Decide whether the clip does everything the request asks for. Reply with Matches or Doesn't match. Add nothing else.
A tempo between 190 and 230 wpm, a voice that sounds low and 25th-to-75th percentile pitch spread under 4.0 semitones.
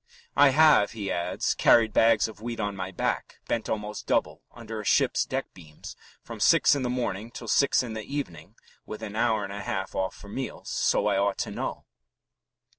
Matches